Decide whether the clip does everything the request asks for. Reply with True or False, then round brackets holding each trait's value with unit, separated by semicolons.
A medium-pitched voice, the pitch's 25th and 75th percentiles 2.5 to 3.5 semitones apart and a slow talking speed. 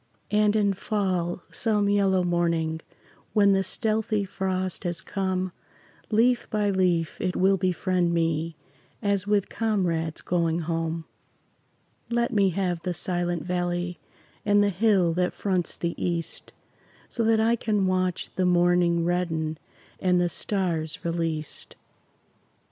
True (180 Hz; 2.9 semitones; 130 wpm)